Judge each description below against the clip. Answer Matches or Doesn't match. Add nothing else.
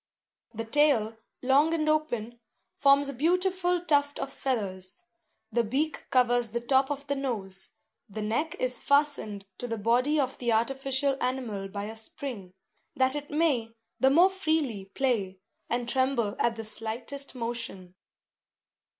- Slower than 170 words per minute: Matches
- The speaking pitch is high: Matches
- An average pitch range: Matches